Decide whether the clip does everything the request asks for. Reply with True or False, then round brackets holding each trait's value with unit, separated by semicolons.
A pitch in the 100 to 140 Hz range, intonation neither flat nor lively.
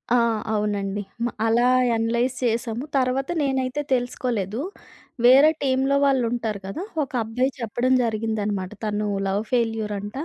False (235 Hz; 3.5 semitones)